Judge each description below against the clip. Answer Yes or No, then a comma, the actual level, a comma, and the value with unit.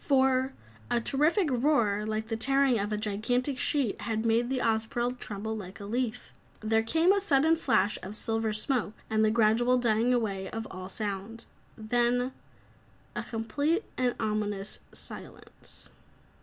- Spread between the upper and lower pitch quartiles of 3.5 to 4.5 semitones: No, average, 3.1 semitones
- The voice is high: Yes, high, 230 Hz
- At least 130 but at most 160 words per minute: Yes, average, 150 wpm